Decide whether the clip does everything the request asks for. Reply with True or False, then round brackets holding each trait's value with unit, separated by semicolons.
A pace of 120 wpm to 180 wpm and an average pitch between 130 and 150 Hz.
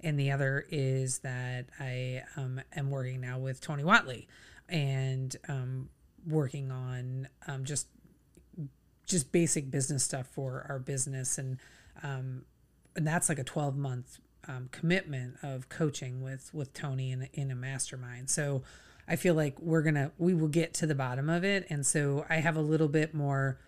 True (165 wpm; 140 Hz)